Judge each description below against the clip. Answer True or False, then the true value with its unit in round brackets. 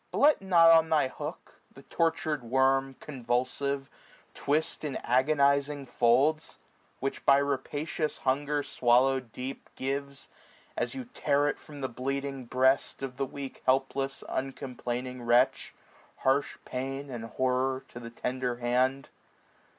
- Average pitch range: False (1.8 semitones)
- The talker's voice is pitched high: False (135 Hz)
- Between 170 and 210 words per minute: False (135 wpm)